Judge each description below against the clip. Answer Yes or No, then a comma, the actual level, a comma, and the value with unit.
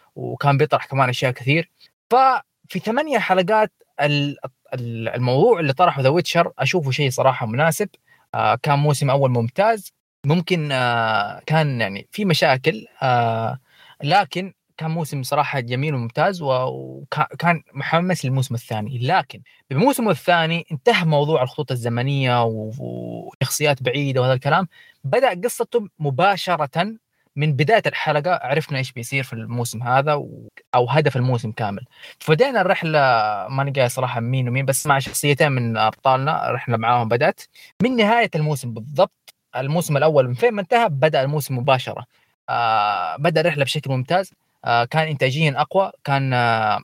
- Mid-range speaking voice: Yes, medium, 145 Hz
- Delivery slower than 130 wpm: No, fast, 135 wpm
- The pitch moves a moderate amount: Yes, average, 5.0 semitones